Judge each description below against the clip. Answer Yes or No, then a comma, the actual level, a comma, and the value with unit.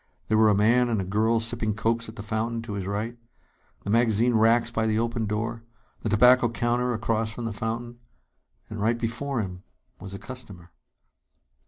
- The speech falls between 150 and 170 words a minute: No, average, 185 wpm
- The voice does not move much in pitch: Yes, narrow, 1.6 semitones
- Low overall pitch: Yes, low, 115 Hz